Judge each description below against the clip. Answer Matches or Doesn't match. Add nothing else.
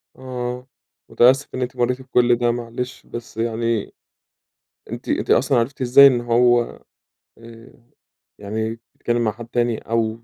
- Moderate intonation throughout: Doesn't match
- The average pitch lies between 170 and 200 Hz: Doesn't match